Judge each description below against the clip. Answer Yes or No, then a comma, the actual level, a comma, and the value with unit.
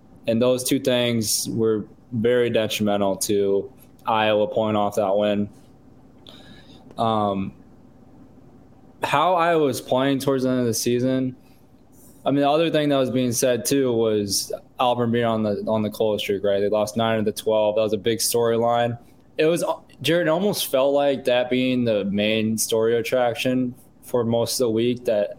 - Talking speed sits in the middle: Yes, average, 175 wpm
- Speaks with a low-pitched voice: Yes, low, 115 Hz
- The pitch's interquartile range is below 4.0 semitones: Yes, average, 3.0 semitones